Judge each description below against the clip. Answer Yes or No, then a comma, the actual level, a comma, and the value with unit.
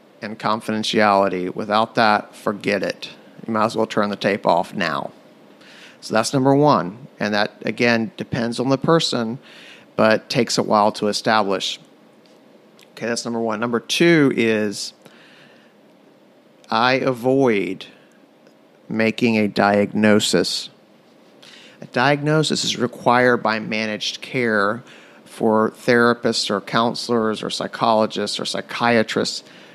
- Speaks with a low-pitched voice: Yes, low, 110 Hz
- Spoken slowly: Yes, slow, 120 wpm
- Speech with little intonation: Yes, narrow, 2.2 semitones